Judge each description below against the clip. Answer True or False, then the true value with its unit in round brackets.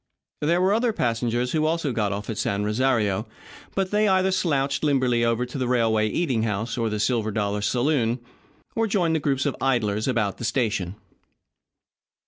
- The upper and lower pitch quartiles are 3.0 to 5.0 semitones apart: False (5.6 semitones)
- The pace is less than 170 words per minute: False (175 wpm)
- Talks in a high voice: False (125 Hz)